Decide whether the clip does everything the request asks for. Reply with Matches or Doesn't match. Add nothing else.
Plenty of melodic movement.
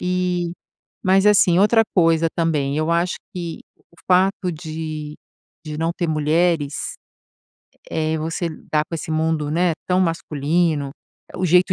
Doesn't match